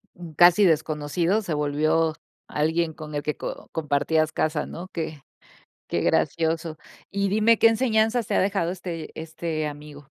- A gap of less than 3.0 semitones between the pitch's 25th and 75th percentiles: No, average, 3.3 semitones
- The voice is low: No, medium, 160 Hz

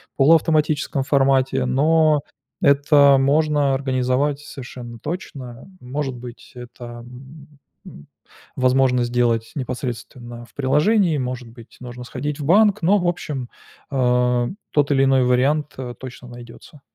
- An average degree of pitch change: Yes, average, 3.0 semitones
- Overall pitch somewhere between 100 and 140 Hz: Yes, low, 135 Hz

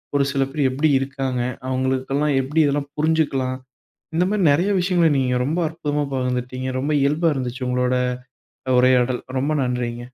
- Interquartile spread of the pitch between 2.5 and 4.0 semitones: Yes, average, 2.8 semitones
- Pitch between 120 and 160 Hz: Yes, low, 135 Hz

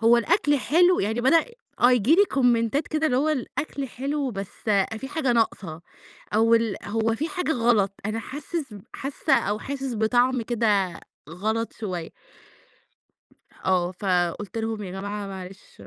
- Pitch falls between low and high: No, high, 230 Hz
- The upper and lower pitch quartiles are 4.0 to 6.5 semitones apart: Yes, average, 5.1 semitones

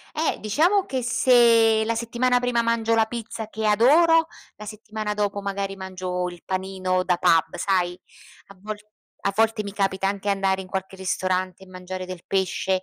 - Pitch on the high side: Yes, high, 200 Hz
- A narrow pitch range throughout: No, average, 3.4 semitones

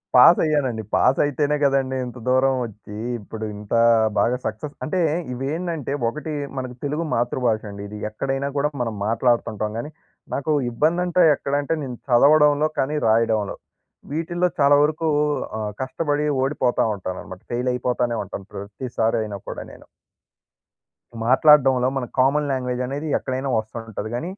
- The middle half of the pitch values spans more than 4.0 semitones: Yes, average, 4.4 semitones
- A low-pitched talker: Yes, low, 130 Hz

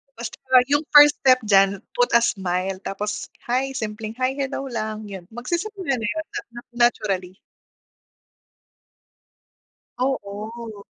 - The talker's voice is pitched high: Yes, high, 225 Hz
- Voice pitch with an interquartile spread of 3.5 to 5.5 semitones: Yes, average, 4.4 semitones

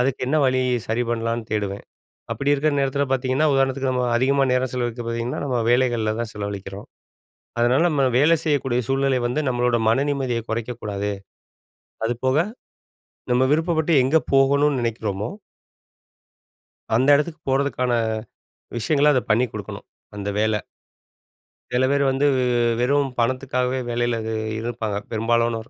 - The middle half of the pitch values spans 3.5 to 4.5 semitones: No, average, 2.8 semitones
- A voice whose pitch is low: Yes, low, 125 Hz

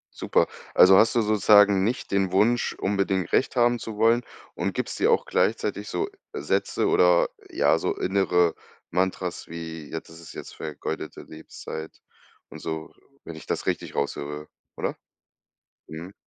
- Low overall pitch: Yes, very low, 95 Hz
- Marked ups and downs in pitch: Yes, wide, 6.2 semitones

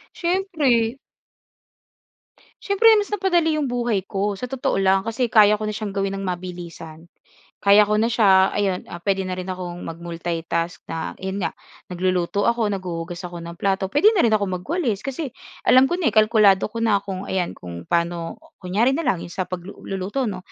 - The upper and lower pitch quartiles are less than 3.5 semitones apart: No, average, 4.7 semitones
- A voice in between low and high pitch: No, high, 195 Hz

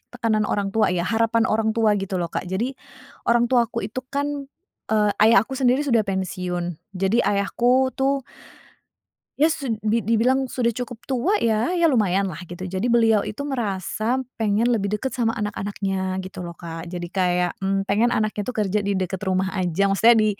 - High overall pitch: Yes, high, 215 Hz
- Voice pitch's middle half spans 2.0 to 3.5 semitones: No, average, 3.9 semitones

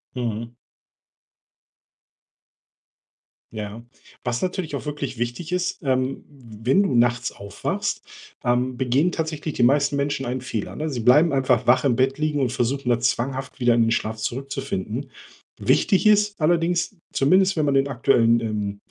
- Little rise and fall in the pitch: No, average, 3.8 semitones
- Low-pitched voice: Yes, low, 130 Hz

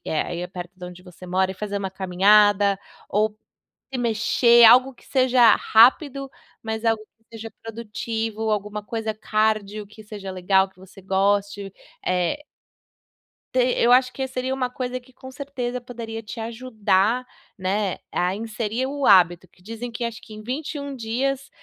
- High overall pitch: Yes, high, 220 Hz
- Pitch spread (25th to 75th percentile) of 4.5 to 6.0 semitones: No, average, 3.8 semitones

